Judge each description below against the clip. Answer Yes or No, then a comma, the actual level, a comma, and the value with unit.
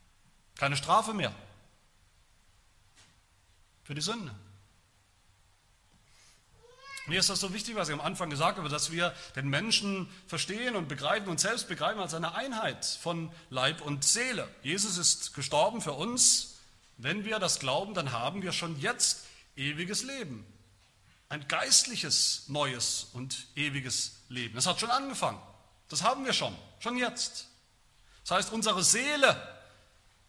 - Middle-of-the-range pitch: Yes, medium, 150 Hz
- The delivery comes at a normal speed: Yes, average, 140 wpm